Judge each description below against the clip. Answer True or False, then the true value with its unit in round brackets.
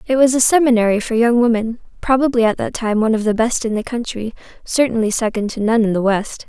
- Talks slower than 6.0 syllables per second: False (6.2 syllables/s)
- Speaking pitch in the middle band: False (230 Hz)